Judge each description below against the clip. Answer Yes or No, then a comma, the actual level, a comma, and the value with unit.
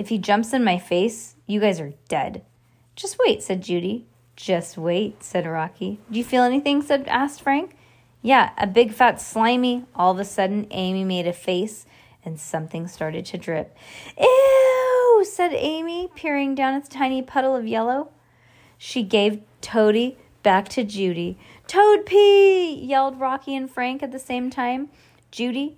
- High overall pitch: Yes, high, 240 Hz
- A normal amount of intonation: No, wide, 6.7 semitones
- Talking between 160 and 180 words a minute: Yes, average, 165 wpm